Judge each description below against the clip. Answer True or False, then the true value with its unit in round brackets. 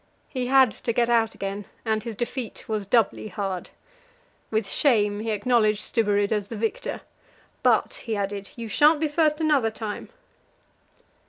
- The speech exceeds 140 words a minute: True (155 wpm)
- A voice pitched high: True (220 Hz)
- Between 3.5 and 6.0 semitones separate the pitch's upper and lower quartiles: False (3.1 semitones)